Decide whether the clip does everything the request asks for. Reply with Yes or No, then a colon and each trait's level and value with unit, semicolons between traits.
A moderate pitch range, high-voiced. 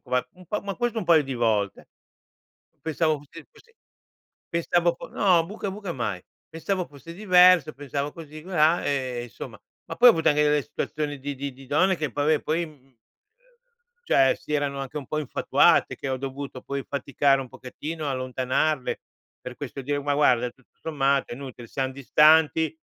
No: average, 3.5 semitones; medium, 145 Hz